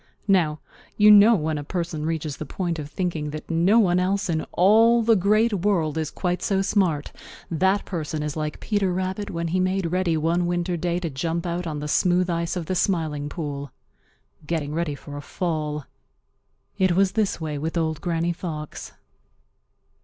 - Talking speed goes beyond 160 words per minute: Yes, average, 180 wpm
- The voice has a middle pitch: Yes, medium, 170 Hz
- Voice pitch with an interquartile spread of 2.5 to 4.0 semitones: Yes, average, 3.3 semitones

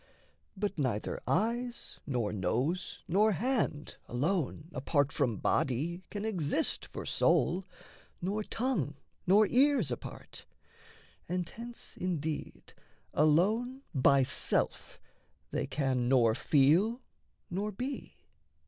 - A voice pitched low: No, medium, 175 Hz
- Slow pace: Yes, slow, 105 wpm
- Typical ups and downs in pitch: No, wide, 7.6 semitones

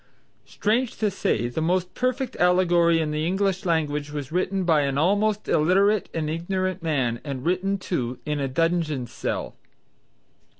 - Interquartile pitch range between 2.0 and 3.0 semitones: No, average, 4.2 semitones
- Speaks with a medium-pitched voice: Yes, medium, 170 Hz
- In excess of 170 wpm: No, average, 155 wpm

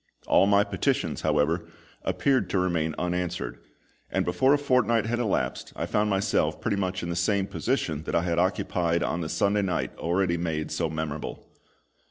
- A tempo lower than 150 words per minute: No, average, 175 wpm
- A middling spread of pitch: Yes, average, 3.4 semitones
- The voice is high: No, very low, 90 Hz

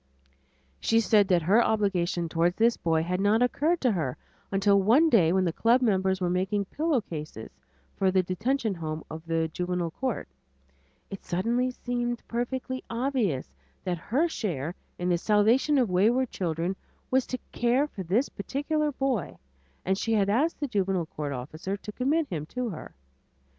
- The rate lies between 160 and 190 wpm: Yes, average, 165 wpm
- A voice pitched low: No, high, 200 Hz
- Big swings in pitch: Yes, wide, 5.8 semitones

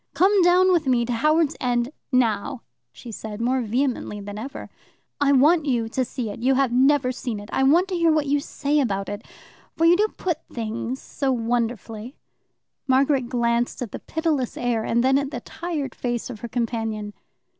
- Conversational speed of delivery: Yes, average, 190 wpm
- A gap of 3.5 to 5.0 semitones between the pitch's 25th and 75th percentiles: Yes, average, 3.8 semitones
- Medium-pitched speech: No, very high, 255 Hz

